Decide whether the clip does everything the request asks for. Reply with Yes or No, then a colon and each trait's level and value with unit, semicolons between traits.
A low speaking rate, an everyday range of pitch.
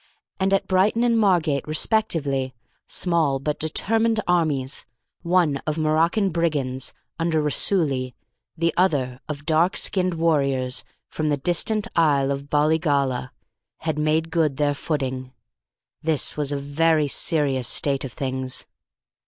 Yes: slow, 130 wpm; average, 3.5 semitones